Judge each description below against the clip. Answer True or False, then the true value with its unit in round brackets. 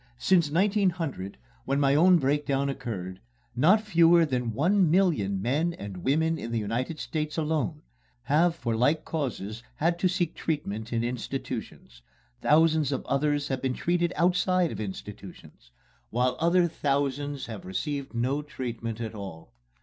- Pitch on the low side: False (145 Hz)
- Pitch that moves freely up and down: True (5.9 semitones)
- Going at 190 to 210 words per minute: False (145 wpm)